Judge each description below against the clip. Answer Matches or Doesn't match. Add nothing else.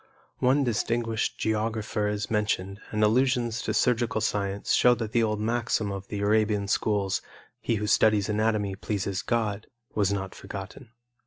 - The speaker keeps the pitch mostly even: Matches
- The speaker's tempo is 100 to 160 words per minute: Matches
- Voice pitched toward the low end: Matches